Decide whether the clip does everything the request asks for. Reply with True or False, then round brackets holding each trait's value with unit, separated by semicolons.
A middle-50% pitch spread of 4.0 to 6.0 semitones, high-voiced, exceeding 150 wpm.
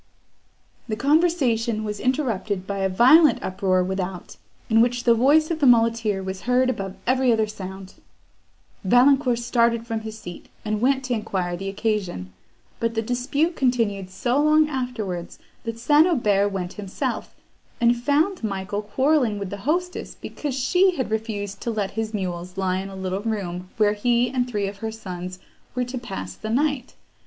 True (4.5 semitones; 225 Hz; 170 wpm)